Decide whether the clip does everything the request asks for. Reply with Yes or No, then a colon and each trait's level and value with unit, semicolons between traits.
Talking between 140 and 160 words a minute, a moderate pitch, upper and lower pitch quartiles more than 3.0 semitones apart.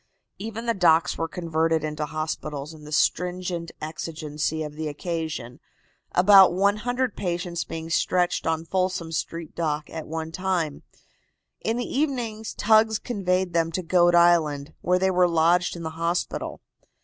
No: average, 150 wpm; medium, 170 Hz; average, 2.7 semitones